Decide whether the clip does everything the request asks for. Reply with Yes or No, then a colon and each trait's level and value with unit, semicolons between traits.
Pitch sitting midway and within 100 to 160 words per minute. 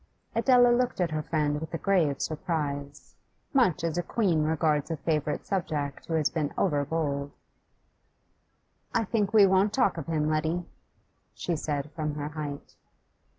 Yes: medium, 160 Hz; average, 155 wpm